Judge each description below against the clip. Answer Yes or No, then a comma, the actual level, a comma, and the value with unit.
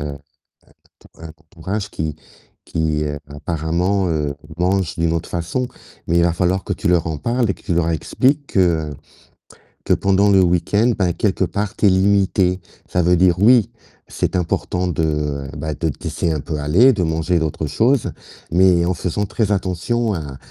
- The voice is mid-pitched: No, very low, 90 Hz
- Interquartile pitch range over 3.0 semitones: Yes, average, 3.5 semitones